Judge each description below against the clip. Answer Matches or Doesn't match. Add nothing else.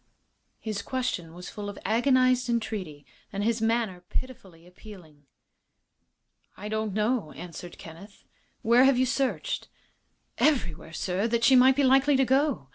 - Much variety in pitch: Matches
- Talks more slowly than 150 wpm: Matches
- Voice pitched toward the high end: Matches